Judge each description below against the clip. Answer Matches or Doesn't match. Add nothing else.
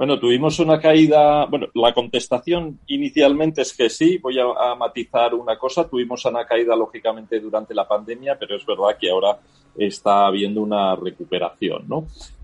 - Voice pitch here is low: Matches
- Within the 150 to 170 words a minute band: Matches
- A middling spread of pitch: Doesn't match